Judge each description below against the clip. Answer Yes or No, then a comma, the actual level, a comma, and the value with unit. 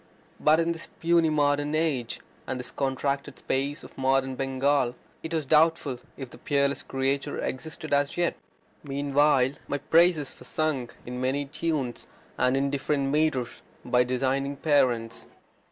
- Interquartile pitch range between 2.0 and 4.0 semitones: Yes, narrow, 2.5 semitones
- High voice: No, medium, 140 Hz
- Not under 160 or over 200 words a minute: No, average, 145 wpm